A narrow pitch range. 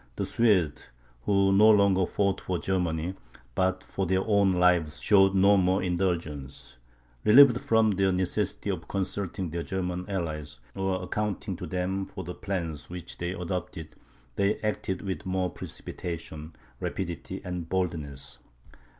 Yes: narrow, 2.1 semitones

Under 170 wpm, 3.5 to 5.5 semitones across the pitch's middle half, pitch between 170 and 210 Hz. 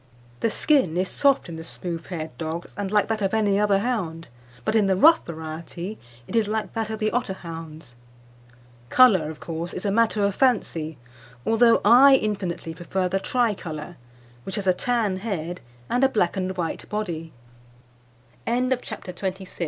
Yes: average, 155 wpm; average, 5.2 semitones; high, 190 Hz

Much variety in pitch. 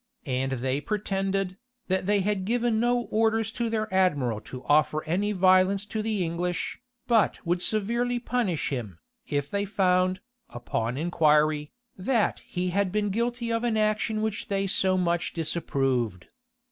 Yes: wide, 5.7 semitones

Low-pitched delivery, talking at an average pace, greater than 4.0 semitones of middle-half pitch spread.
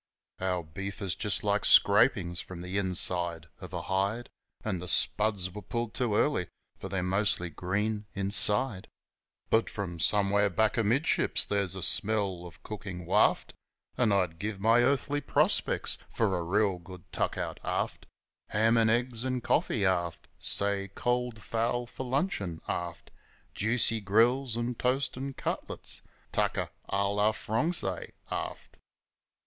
No: low, 100 Hz; average, 145 wpm; average, 3.7 semitones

